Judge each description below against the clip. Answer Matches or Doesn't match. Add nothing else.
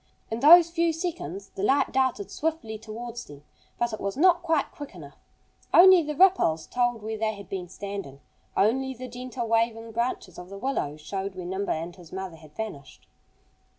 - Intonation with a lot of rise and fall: Matches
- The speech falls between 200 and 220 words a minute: Doesn't match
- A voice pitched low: Doesn't match